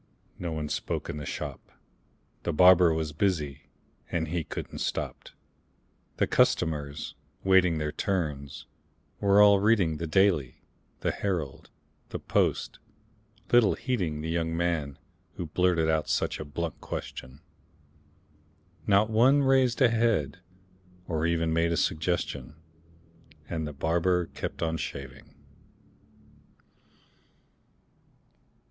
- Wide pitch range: No, average, 3.8 semitones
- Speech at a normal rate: No, slow, 115 wpm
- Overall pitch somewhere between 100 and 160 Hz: No, very low, 85 Hz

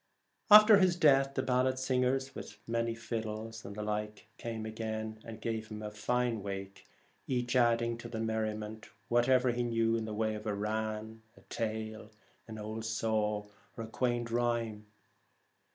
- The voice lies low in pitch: Yes, low, 110 Hz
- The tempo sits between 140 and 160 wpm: Yes, average, 150 wpm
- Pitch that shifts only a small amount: Yes, narrow, 1.9 semitones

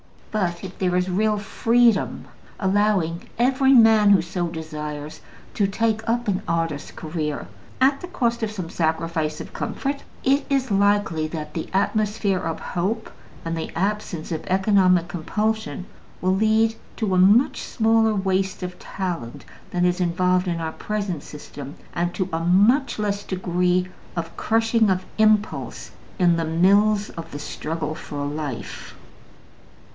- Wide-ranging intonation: No, average, 4.4 semitones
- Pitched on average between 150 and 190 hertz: Yes, medium, 185 Hz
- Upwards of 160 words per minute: No, average, 150 wpm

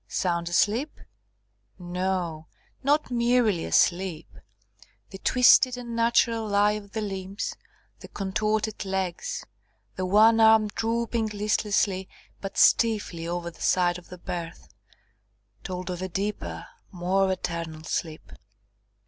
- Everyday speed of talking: No, slow, 115 wpm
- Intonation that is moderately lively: Yes, average, 3.9 semitones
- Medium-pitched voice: No, high, 195 Hz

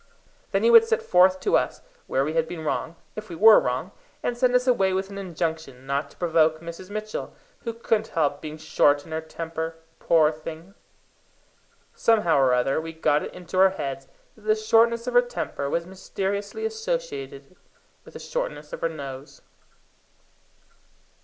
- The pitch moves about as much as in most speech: No, wide, 6.1 semitones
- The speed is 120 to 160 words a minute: No, average, 175 wpm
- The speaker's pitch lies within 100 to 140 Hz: No, medium, 175 Hz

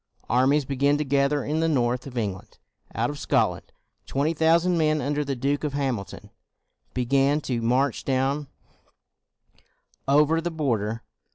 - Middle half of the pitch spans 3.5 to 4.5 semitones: No, average, 2.8 semitones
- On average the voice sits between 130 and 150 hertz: Yes, medium, 140 Hz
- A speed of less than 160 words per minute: Yes, average, 145 wpm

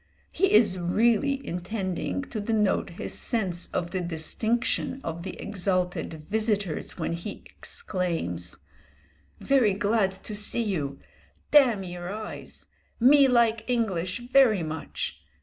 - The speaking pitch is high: Yes, high, 205 Hz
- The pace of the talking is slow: Yes, slow, 115 wpm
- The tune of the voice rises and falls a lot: No, average, 4.7 semitones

